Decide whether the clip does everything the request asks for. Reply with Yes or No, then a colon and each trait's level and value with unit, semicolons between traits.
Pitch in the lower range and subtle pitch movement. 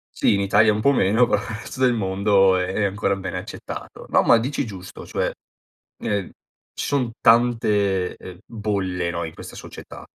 No: low, 100 Hz; average, 3.1 semitones